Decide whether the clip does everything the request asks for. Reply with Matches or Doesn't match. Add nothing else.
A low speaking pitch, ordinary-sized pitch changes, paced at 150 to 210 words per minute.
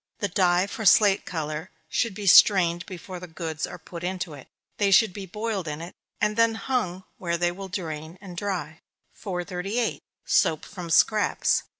Doesn't match